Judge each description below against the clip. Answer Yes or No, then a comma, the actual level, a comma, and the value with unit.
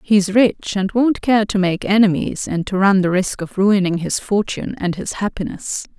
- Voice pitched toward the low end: No, high, 195 Hz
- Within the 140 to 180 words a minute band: No, average, 200 wpm